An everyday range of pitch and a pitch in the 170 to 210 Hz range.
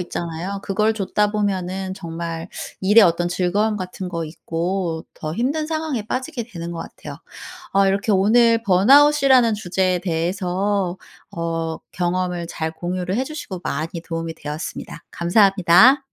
Yes: average, 3.8 semitones; medium, 185 Hz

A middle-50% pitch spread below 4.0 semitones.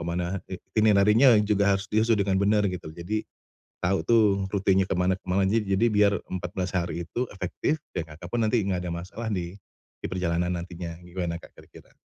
Yes: average, 2.9 semitones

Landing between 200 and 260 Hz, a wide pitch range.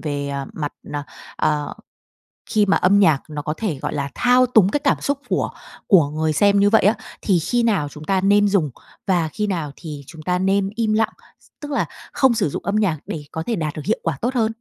No: high, 190 Hz; wide, 5.7 semitones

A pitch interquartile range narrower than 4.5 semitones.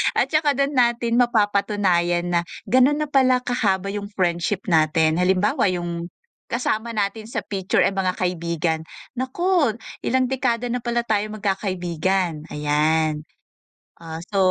No: wide, 5.6 semitones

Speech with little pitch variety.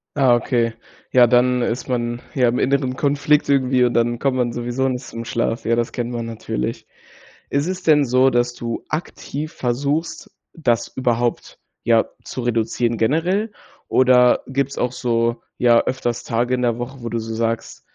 Yes: narrow, 2.1 semitones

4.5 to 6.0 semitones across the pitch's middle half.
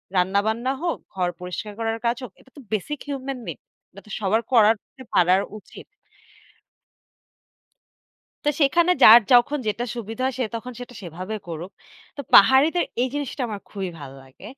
Yes: average, 5.3 semitones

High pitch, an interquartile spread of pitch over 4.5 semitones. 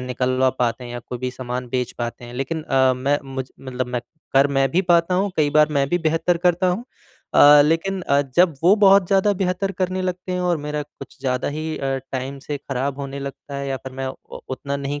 No: medium, 140 Hz; average, 5.0 semitones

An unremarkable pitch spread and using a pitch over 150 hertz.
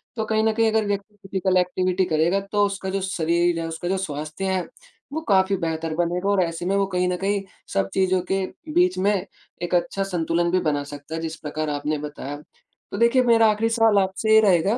Yes: average, 3.5 semitones; medium, 185 Hz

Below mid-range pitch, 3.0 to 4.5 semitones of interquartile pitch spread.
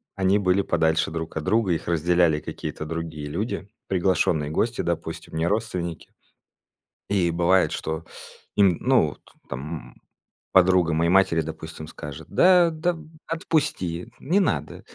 Yes: very low, 85 Hz; average, 3.7 semitones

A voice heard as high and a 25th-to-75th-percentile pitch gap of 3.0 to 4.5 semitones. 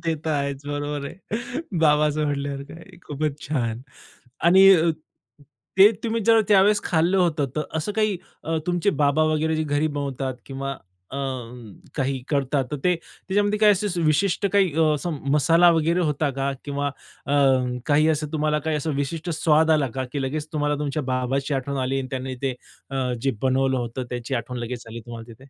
No: medium, 150 Hz; average, 3.4 semitones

